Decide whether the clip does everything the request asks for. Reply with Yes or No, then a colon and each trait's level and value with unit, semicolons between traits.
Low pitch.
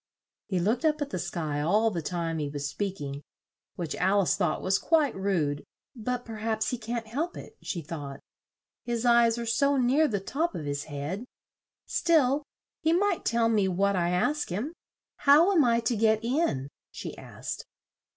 No: high, 220 Hz